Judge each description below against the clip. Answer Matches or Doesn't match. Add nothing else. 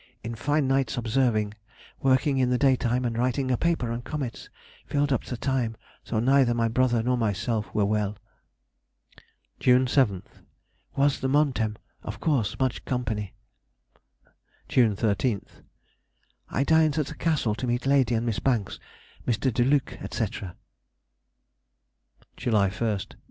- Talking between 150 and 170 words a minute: Doesn't match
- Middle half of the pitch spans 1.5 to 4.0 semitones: Matches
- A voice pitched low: Matches